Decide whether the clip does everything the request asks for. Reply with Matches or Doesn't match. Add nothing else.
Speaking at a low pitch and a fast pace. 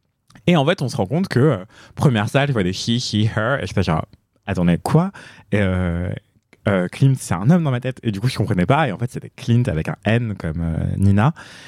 Matches